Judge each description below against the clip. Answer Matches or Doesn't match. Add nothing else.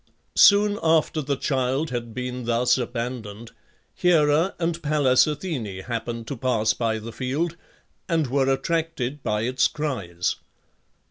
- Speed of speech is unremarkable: Doesn't match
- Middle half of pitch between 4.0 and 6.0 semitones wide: Matches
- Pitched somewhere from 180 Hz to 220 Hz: Doesn't match